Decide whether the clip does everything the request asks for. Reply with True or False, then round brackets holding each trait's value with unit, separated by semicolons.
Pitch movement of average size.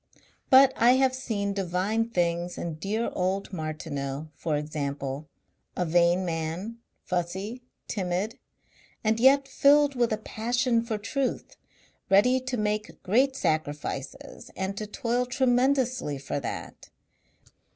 False (6.4 semitones)